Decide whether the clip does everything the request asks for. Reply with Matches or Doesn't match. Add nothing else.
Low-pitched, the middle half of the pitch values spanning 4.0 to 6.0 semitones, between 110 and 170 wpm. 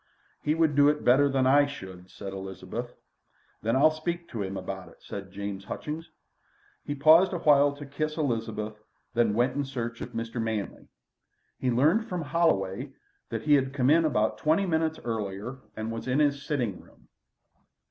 Doesn't match